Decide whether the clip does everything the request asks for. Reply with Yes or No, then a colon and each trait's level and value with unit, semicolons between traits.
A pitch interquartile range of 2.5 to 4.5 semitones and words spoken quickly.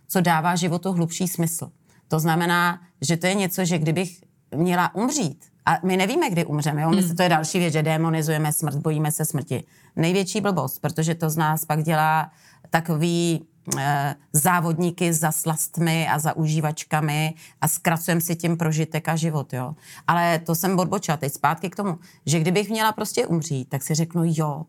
No: narrow, 2.1 semitones; fast, 180 wpm